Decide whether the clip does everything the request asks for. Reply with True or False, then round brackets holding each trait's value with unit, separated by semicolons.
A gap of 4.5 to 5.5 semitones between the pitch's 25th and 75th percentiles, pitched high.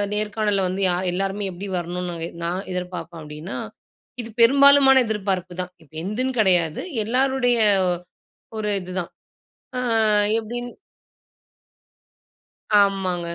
False (4.0 semitones; 195 Hz)